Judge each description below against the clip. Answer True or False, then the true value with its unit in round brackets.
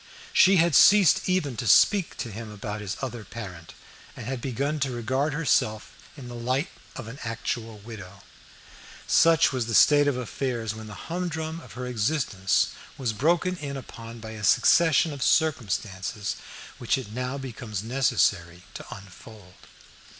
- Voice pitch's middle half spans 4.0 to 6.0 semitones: True (4.9 semitones)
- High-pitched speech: False (120 Hz)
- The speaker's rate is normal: True (155 wpm)